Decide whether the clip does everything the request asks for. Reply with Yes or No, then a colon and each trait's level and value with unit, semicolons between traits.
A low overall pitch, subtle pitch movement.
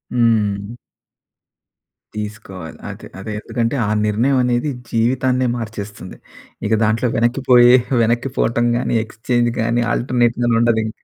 Yes: low, 115 Hz; narrow, 2.1 semitones